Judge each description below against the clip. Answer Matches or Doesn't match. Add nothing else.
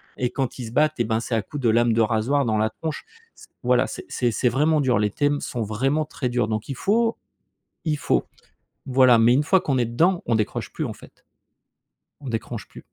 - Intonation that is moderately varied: Matches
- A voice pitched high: Doesn't match